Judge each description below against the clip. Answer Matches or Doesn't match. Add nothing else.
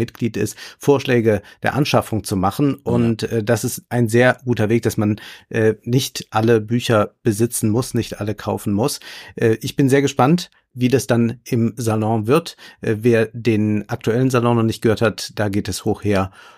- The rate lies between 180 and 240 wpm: Matches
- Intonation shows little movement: Matches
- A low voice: Matches